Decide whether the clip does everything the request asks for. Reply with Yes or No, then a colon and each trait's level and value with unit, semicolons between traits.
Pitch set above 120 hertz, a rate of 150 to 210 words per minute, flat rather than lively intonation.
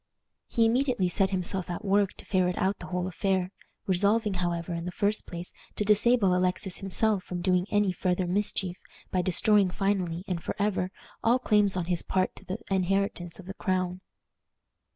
Yes: medium, 185 Hz; average, 175 wpm; narrow, 2.1 semitones